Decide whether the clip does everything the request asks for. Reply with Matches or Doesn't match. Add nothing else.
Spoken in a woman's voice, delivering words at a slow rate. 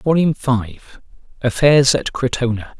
Doesn't match